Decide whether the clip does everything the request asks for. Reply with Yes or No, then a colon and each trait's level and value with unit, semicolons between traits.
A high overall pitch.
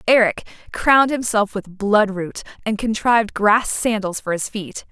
Yes: high, 215 Hz